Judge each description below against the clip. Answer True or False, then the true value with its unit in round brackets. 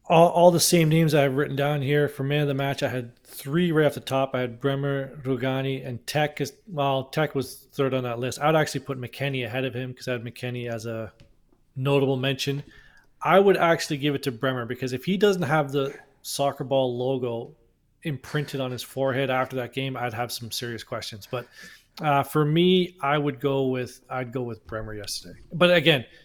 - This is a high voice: False (135 Hz)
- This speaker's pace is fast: True (215 wpm)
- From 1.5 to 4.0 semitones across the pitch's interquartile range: True (2.7 semitones)